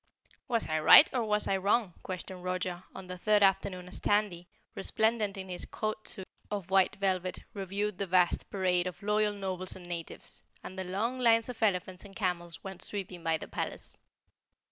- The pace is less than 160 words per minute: No, average, 185 wpm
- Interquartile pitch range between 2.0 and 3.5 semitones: Yes, narrow, 2.4 semitones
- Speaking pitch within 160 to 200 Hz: Yes, high, 190 Hz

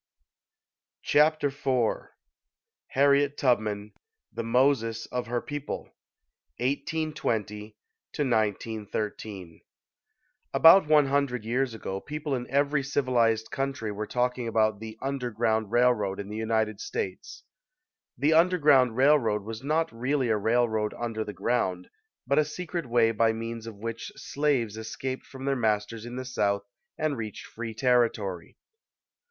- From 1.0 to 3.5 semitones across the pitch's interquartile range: No, average, 4.1 semitones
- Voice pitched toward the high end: No, low, 120 Hz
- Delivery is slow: Yes, slow, 125 wpm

